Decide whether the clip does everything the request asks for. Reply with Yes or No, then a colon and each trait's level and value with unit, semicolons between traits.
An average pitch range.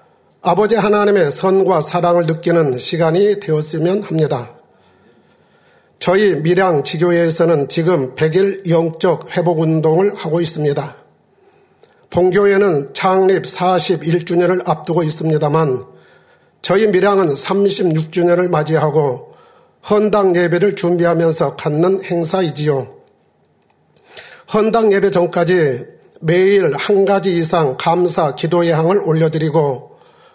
Yes: average, 3.1 semitones